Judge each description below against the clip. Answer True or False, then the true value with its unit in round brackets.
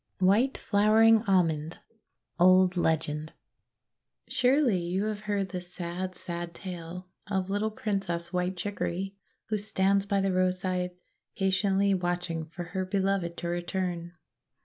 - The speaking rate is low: True (130 wpm)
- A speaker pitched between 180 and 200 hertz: True (185 Hz)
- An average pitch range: False (2.2 semitones)